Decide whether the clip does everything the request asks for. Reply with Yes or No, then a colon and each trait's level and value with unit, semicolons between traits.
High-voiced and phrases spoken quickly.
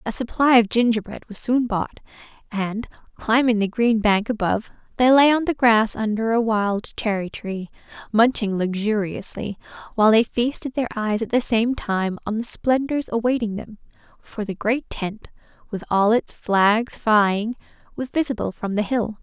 No: high, 220 Hz; average, 165 wpm